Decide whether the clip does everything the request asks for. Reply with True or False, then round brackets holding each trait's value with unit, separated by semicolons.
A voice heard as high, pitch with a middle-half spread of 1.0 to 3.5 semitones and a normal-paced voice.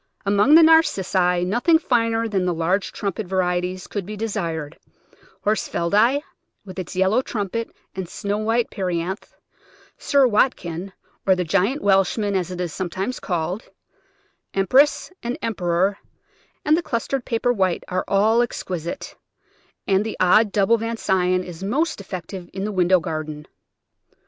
False (195 Hz; 4.1 semitones; 145 wpm)